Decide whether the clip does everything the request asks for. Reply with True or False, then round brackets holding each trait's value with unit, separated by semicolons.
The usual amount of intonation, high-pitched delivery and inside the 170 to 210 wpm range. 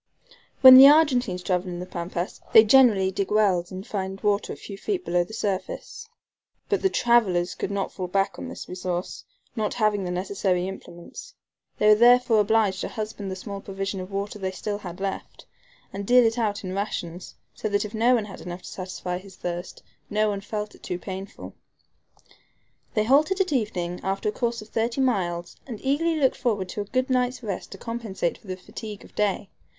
True (3.7 semitones; 205 Hz; 200 wpm)